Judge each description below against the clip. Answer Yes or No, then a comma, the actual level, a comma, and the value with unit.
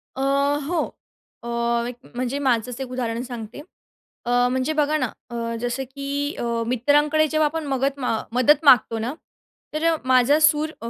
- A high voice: Yes, very high, 265 Hz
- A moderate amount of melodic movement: Yes, average, 3.5 semitones